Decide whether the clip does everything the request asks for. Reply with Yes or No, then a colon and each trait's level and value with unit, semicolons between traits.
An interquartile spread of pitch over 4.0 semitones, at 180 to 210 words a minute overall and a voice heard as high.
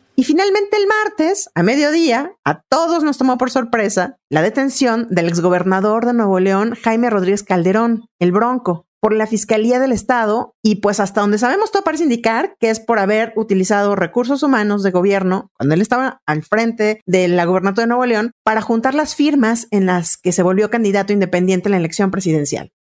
Yes: average, 4.6 semitones; fast, 190 wpm; high, 220 Hz